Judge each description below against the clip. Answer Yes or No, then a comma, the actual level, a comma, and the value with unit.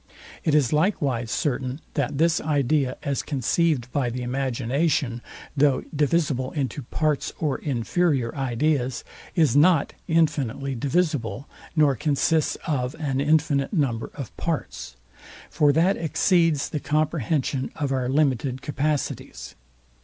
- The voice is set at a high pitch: No, medium, 140 Hz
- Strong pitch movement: No, average, 3.1 semitones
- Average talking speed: No, slow, 120 wpm